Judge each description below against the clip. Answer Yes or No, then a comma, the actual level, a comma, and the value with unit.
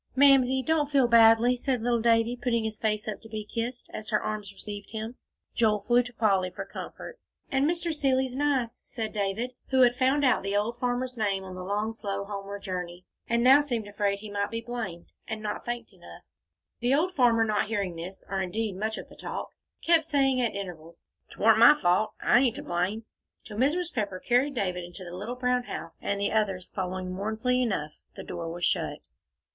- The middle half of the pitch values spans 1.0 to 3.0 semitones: No, average, 3.9 semitones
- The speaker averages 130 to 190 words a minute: No, fast, 205 wpm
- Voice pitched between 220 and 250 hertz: Yes, high, 225 Hz